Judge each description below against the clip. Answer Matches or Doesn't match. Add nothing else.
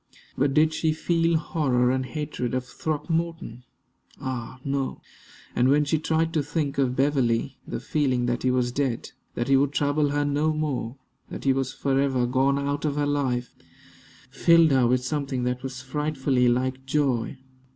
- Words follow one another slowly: Doesn't match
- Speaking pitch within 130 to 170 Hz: Matches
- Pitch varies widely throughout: Doesn't match